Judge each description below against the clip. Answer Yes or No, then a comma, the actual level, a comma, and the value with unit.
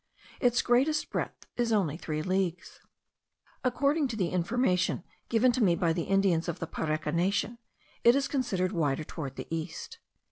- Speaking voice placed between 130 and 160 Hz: No, medium, 185 Hz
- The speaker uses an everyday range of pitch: No, wide, 6.4 semitones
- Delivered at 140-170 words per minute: Yes, average, 150 wpm